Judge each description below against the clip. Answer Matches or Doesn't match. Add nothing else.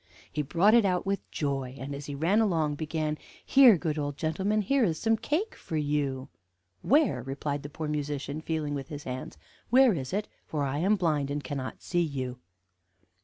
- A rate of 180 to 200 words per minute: Matches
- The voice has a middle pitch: Matches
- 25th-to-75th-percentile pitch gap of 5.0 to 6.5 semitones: Matches